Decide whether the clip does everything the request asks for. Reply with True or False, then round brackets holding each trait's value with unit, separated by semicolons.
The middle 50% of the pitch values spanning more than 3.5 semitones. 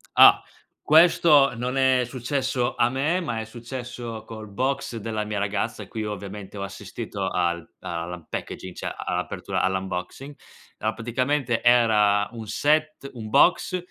True (4.4 semitones)